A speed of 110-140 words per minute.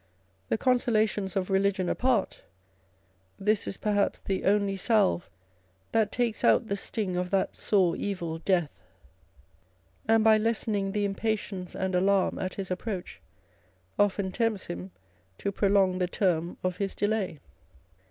Yes: slow, 135 wpm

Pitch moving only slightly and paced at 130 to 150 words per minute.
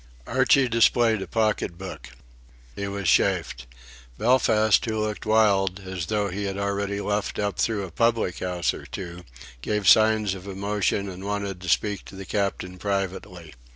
No: narrow, 2.2 semitones; average, 160 wpm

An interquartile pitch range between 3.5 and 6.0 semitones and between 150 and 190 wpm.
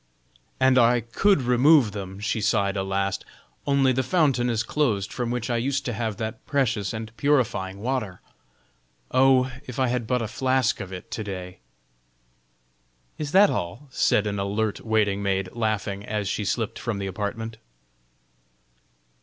Yes: average, 4.2 semitones; average, 160 wpm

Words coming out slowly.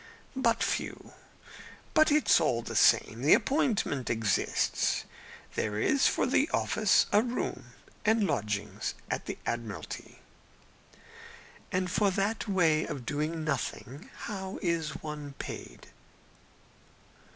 Yes: slow, 115 wpm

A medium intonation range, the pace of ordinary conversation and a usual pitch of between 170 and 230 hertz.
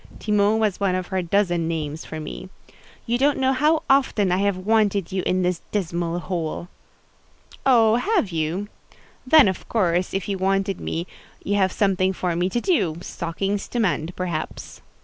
Yes: average, 3.4 semitones; average, 170 wpm; high, 190 Hz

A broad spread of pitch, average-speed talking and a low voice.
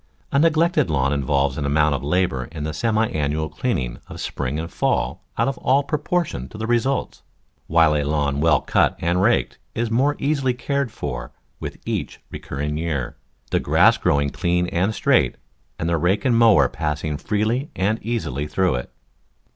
Yes: wide, 8.3 semitones; average, 180 wpm; very low, 85 Hz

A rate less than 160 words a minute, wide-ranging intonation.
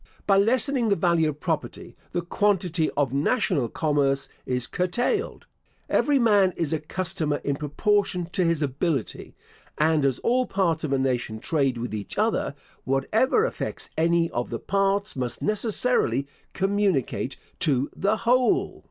Yes: average, 145 wpm; wide, 6.6 semitones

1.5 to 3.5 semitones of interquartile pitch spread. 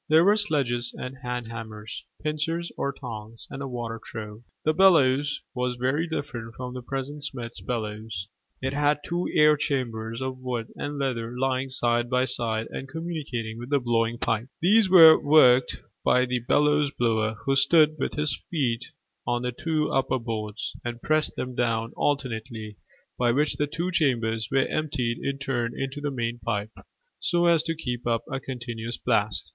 No: average, 3.9 semitones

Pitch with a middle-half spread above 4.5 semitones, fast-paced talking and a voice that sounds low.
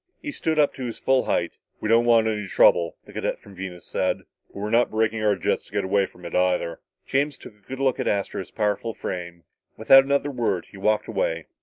Yes: average, 5.2 semitones; fast, 225 wpm; low, 110 Hz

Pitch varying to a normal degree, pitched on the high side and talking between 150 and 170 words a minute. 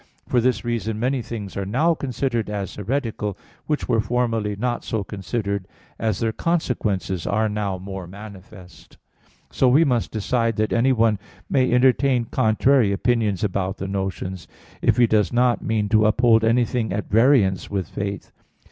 No: average, 3.4 semitones; low, 110 Hz; average, 155 wpm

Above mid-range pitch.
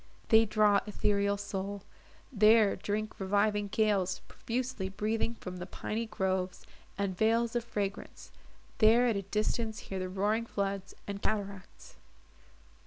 Yes: high, 205 Hz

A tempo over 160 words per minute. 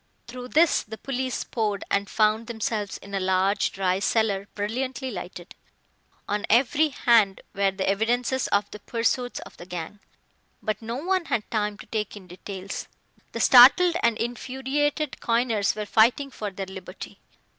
No: average, 155 wpm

